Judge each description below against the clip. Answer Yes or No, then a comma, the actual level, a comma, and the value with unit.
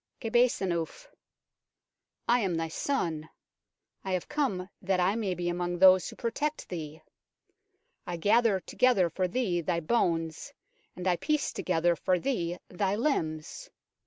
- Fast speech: No, average, 140 wpm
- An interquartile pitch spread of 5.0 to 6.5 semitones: Yes, average, 5.3 semitones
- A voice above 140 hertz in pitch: Yes, medium, 185 Hz